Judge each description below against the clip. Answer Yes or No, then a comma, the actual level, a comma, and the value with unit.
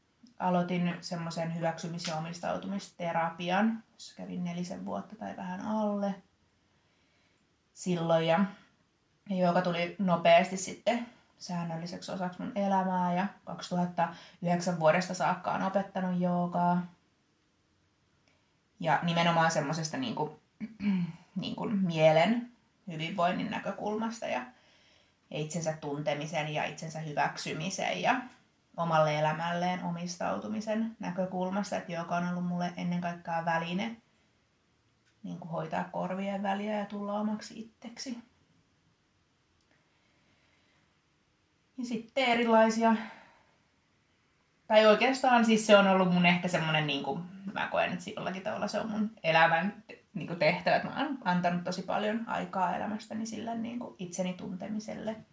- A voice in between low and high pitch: Yes, medium, 180 Hz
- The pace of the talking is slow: No, average, 110 wpm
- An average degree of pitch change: Yes, average, 4.0 semitones